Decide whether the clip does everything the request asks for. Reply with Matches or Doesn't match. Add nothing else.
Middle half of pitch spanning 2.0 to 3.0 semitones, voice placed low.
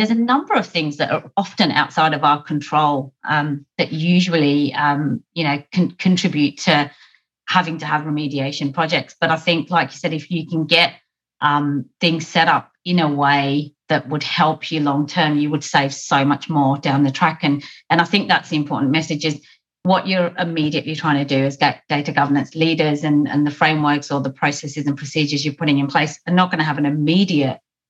Doesn't match